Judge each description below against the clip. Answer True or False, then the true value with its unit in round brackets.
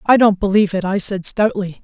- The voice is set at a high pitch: True (200 Hz)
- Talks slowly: False (230 wpm)